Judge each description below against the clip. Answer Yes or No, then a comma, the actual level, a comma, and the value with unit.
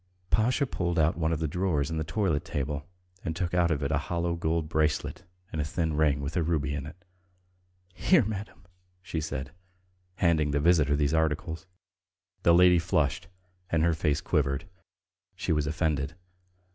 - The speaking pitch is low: Yes, very low, 80 Hz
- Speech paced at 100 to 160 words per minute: No, average, 170 wpm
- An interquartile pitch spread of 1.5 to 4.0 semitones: Yes, narrow, 2.6 semitones